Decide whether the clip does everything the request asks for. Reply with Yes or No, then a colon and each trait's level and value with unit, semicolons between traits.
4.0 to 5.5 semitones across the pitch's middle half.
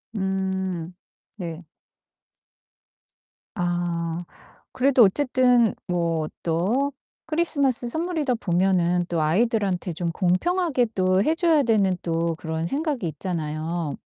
No: wide, 6.8 semitones